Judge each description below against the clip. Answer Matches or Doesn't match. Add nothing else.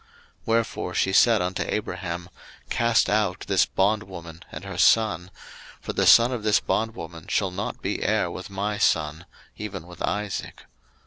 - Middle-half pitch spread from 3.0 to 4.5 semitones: Matches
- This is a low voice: Matches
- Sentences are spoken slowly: Doesn't match